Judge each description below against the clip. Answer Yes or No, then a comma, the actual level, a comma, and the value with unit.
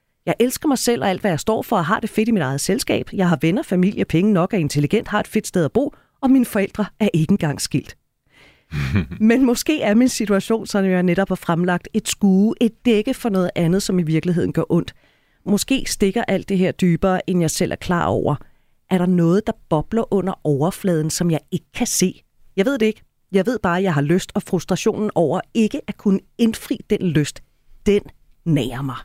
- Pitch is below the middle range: No, high, 195 Hz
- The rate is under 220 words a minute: No, fast, 225 wpm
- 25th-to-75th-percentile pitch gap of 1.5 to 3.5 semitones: No, average, 4.1 semitones